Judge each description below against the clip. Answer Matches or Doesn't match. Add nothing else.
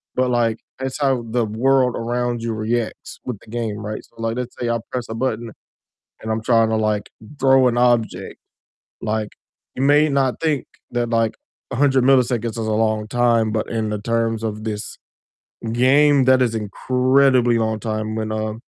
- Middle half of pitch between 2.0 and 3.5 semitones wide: Matches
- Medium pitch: Doesn't match